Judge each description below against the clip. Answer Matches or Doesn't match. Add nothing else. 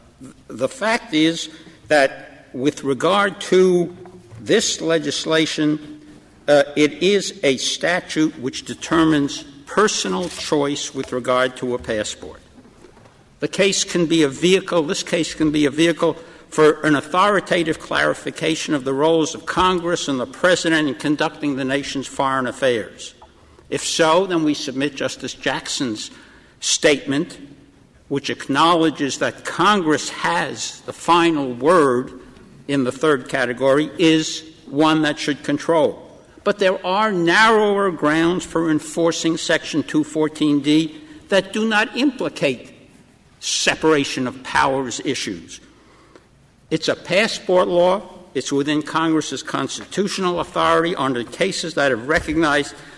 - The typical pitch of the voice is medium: Matches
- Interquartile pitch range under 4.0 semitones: Matches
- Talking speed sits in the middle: Doesn't match